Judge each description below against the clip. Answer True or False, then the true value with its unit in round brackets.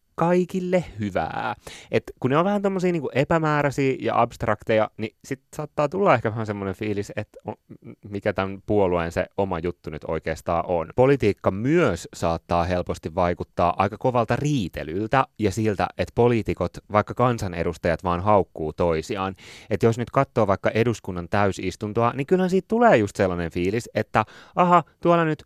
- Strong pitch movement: True (6.6 semitones)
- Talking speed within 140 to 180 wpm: True (150 wpm)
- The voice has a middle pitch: False (110 Hz)